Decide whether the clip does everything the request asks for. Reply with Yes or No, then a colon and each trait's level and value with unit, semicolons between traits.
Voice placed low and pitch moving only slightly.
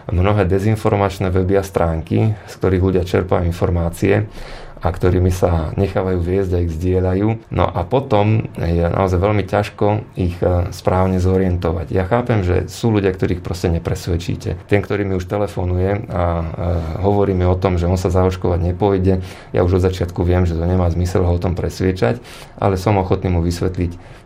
Yes: very low, 95 Hz; narrow, 2.3 semitones